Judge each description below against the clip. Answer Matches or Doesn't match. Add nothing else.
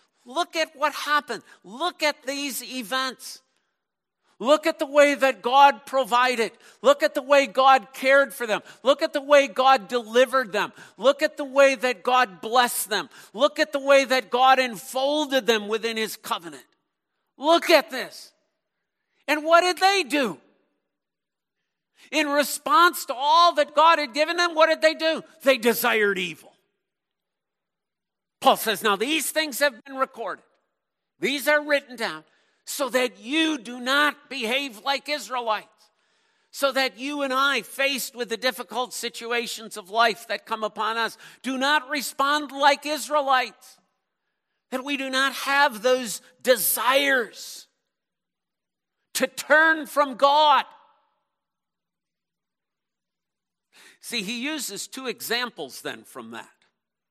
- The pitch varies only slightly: Doesn't match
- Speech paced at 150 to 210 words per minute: Doesn't match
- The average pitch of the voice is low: Doesn't match